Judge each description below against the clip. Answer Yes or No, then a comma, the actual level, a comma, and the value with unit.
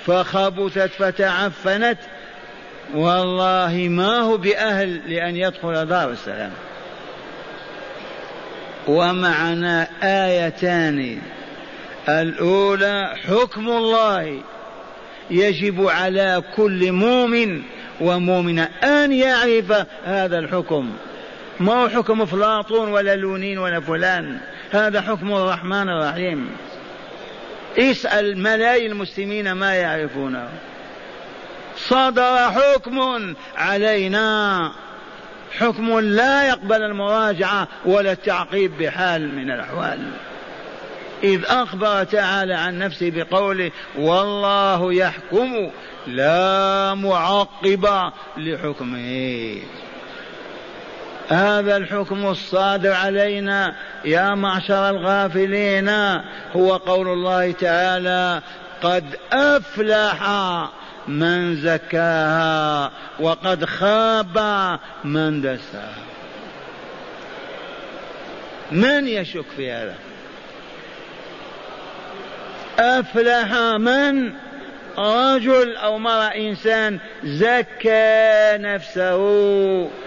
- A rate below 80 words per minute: Yes, average, 70 wpm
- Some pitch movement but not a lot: Yes, average, 3.3 semitones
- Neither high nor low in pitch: No, high, 195 Hz